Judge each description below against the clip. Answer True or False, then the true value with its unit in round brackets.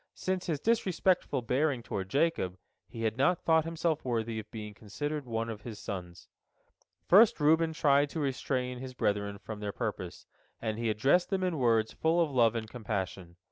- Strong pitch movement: True (6.6 semitones)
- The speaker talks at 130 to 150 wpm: False (180 wpm)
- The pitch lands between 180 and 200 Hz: False (125 Hz)